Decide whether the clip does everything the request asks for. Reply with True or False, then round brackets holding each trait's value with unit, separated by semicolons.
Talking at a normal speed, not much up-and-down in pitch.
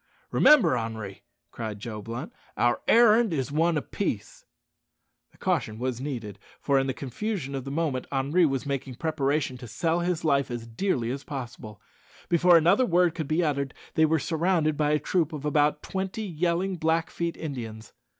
False (170 wpm; 5.0 semitones)